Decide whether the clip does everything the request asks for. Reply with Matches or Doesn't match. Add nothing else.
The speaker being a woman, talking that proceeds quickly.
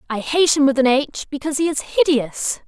Matches